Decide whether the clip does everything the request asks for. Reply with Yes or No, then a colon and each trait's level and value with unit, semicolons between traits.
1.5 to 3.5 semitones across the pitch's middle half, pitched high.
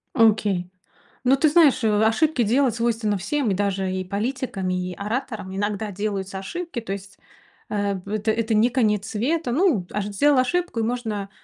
No: average, 4.1 semitones; high, 215 Hz